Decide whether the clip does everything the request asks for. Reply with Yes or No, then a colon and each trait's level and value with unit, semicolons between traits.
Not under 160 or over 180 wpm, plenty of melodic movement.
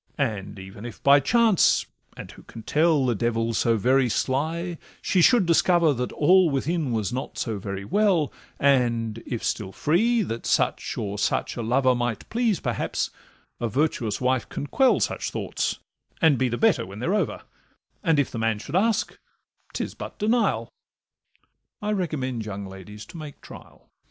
Yes: average, 165 wpm; wide, 7.0 semitones